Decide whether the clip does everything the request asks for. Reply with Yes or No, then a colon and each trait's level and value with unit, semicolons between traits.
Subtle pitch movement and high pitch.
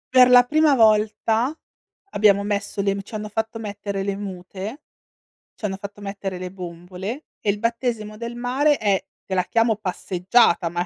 No: average, 3.0 semitones; high, 210 Hz